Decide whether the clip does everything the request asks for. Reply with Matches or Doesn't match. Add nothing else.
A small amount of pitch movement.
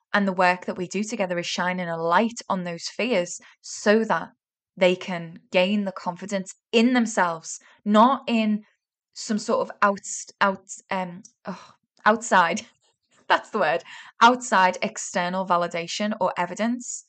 Doesn't match